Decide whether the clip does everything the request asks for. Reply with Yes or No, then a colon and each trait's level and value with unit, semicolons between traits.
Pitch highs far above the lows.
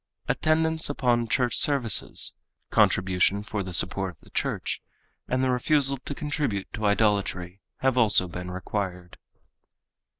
Yes: wide, 6.0 semitones